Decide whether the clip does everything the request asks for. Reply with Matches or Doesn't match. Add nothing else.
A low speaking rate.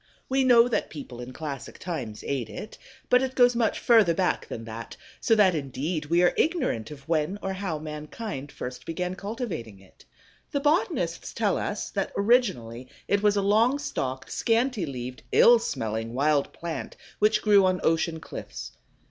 Doesn't match